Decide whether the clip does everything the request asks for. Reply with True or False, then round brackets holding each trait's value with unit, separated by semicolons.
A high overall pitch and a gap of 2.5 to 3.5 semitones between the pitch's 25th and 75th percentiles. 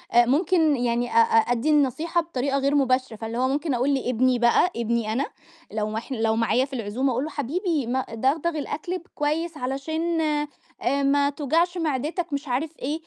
False (275 Hz; 4.2 semitones)